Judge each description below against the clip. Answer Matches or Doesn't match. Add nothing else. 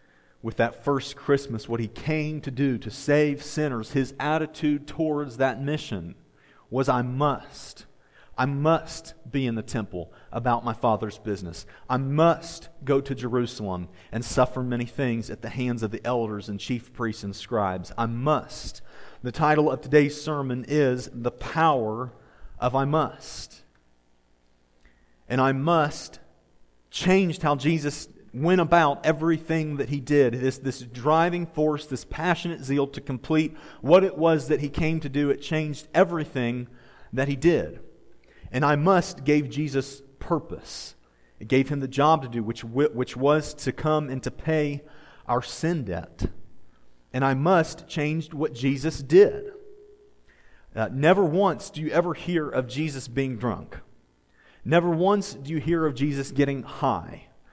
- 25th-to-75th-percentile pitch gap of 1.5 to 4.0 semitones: Doesn't match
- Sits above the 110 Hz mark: Matches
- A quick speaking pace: Doesn't match